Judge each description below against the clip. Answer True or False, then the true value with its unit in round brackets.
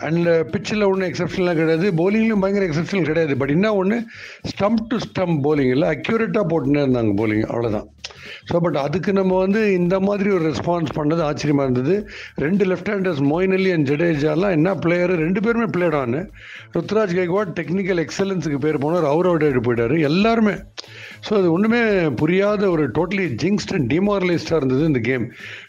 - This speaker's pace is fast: True (155 wpm)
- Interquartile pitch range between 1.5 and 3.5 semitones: False (4.5 semitones)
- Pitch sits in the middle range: True (175 Hz)